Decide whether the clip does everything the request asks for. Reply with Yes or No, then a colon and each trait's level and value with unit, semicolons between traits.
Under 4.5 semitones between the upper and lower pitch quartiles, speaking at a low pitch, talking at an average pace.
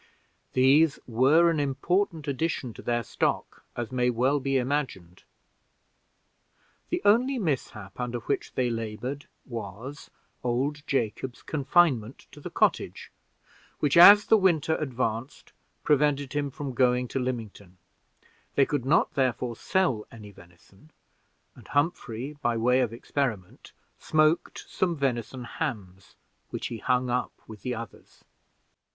No: average, 3.9 semitones; low, 130 Hz; slow, 130 wpm